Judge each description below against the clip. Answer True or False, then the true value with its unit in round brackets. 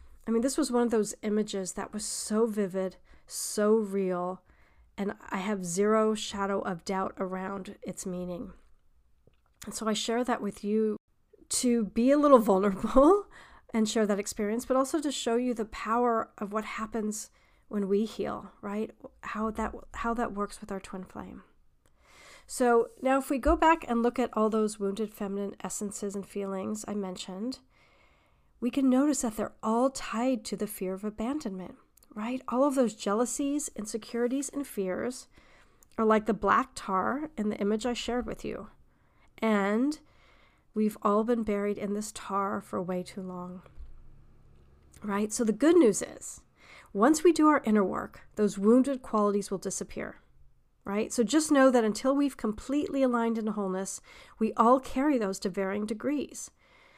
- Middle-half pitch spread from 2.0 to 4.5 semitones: True (3.5 semitones)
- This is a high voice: True (215 Hz)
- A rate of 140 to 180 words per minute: True (170 wpm)